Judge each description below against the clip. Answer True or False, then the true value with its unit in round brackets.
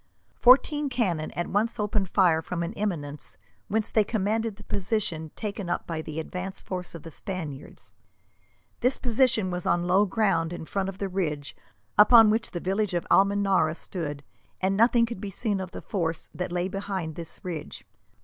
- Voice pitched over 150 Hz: True (190 Hz)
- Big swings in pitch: False (3.8 semitones)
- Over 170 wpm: True (180 wpm)